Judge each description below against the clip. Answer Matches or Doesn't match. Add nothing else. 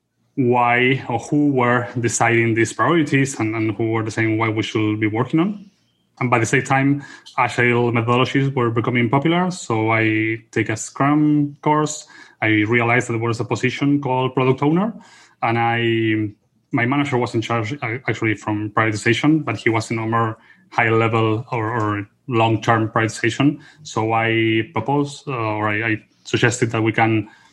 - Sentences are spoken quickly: Doesn't match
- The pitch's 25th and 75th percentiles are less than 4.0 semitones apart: Matches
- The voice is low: Matches